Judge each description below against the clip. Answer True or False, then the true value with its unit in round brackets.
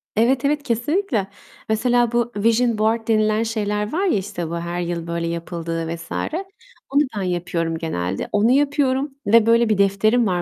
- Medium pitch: False (215 Hz)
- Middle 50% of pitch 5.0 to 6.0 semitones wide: True (5.5 semitones)